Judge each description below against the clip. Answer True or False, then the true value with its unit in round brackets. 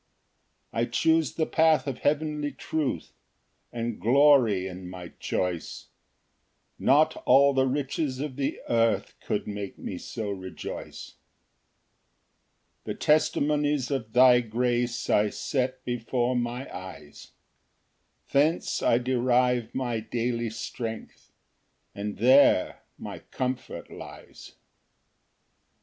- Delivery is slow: True (110 wpm)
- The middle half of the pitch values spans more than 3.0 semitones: True (3.8 semitones)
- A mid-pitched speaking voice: False (125 Hz)